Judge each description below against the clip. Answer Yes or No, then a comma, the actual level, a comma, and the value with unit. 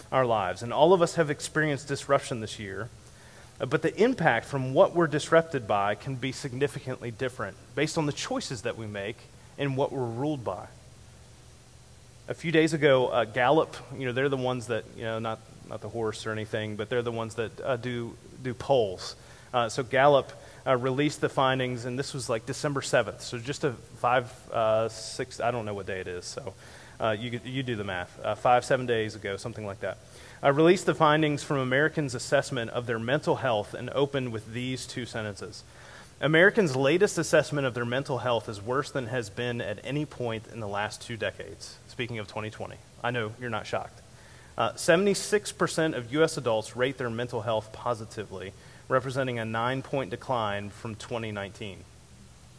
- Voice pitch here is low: Yes, low, 125 Hz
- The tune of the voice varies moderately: Yes, average, 3.8 semitones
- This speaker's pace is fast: No, average, 195 wpm